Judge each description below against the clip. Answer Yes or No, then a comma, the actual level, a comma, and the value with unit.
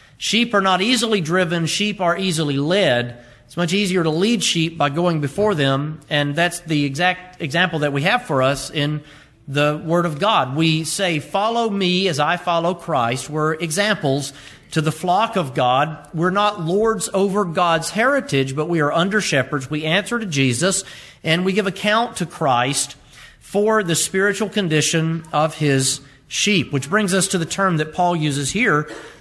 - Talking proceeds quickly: No, average, 180 wpm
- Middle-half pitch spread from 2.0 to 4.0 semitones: No, average, 4.8 semitones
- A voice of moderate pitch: Yes, medium, 165 Hz